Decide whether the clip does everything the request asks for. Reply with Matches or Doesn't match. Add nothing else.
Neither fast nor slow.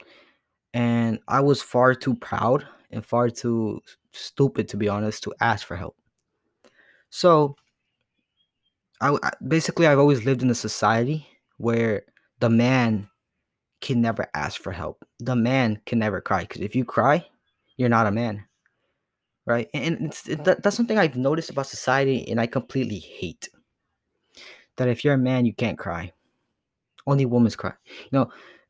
Matches